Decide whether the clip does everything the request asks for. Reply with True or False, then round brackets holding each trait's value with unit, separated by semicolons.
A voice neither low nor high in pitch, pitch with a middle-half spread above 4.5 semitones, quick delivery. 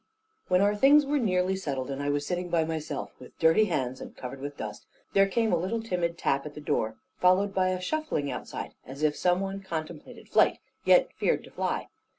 True (175 Hz; 5.2 semitones; 210 wpm)